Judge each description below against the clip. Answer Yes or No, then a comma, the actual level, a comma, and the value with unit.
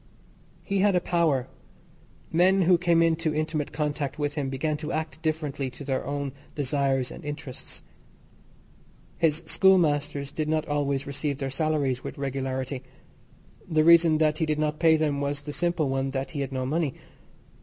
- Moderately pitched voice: Yes, medium, 150 Hz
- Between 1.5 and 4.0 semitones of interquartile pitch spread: Yes, narrow, 2.5 semitones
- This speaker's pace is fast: No, average, 165 wpm